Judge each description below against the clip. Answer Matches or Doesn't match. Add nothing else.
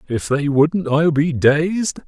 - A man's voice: Matches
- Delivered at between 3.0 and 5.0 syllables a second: Matches